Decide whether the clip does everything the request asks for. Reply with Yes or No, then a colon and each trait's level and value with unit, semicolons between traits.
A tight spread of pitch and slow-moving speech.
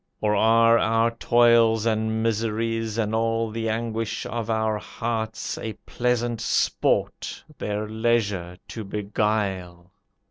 Yes: narrow, 1.3 semitones; slow, 115 wpm